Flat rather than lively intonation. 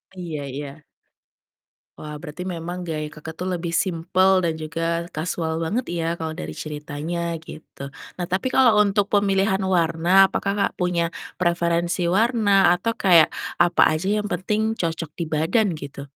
No: average, 3.1 semitones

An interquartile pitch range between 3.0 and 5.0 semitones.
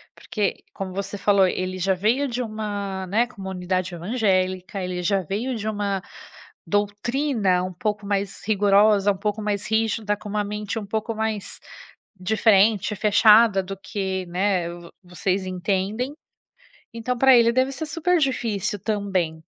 No: narrow, 2.5 semitones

